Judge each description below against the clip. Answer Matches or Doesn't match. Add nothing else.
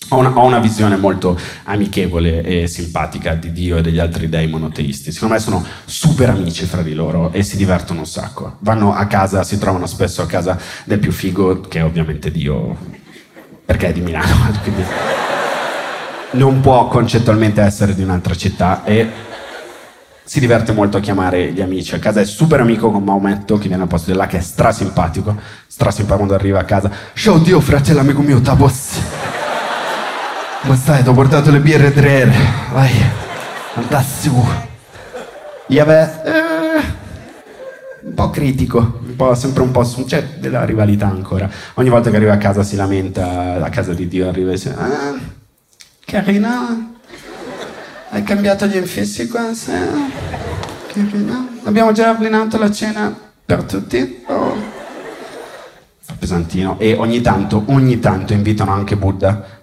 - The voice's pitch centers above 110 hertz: Doesn't match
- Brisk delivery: Doesn't match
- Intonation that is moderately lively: Doesn't match